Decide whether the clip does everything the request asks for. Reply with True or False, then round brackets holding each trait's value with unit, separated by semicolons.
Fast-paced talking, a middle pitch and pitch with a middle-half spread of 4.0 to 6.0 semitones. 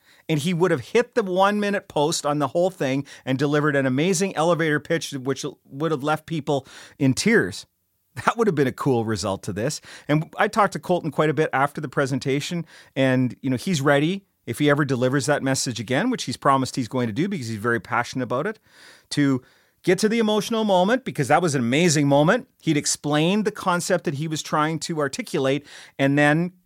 True (215 wpm; 150 Hz; 4.5 semitones)